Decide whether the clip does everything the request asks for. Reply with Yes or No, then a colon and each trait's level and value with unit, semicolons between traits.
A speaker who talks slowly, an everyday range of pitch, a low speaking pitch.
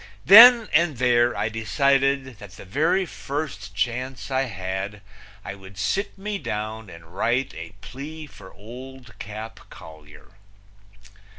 No: slow, 130 wpm; wide, 5.9 semitones; low, 120 Hz